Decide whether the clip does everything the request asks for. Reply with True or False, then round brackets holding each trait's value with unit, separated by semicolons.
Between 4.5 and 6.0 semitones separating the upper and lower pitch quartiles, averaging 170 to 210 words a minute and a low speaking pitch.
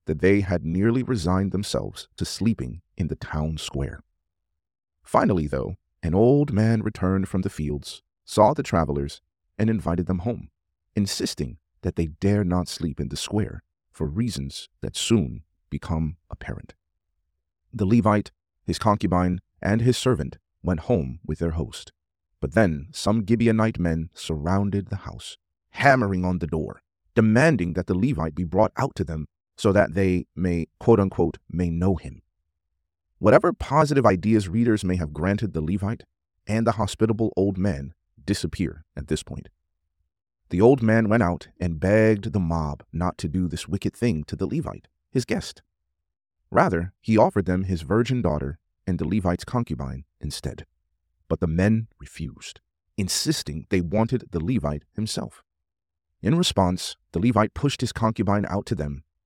False (4.8 semitones; 155 wpm; 90 Hz)